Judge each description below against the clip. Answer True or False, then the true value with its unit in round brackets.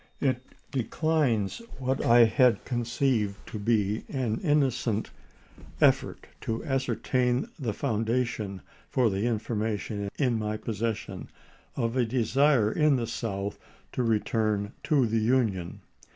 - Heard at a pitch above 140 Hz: False (115 Hz)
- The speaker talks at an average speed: False (115 wpm)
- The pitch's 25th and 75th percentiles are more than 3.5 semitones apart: False (3.2 semitones)